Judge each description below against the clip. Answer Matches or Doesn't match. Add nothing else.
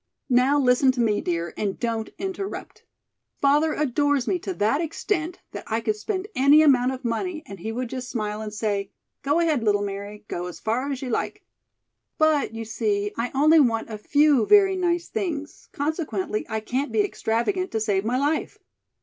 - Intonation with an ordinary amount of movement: Doesn't match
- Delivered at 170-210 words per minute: Matches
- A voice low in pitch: Doesn't match